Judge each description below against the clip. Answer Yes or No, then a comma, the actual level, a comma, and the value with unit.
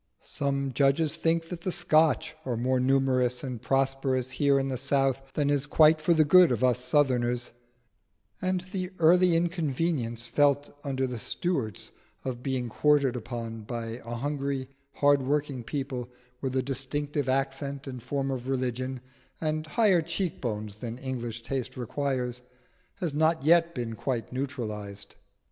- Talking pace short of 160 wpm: Yes, average, 150 wpm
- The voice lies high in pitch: No, low, 135 Hz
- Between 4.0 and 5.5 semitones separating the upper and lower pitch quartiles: No, average, 3.2 semitones